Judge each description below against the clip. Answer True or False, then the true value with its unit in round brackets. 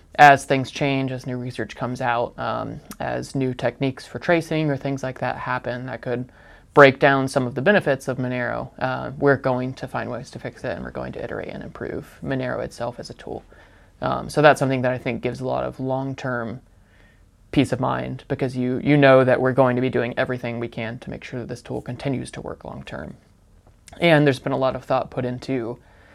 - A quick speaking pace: True (225 wpm)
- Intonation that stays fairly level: True (2.3 semitones)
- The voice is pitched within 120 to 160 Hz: True (130 Hz)